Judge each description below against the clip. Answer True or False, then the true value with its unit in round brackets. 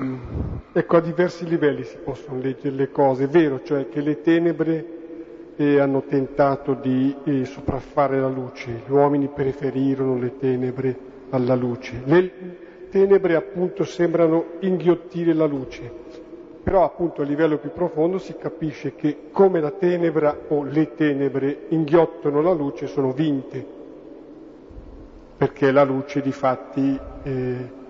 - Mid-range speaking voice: True (145 Hz)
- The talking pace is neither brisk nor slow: True (135 wpm)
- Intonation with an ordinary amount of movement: True (3.7 semitones)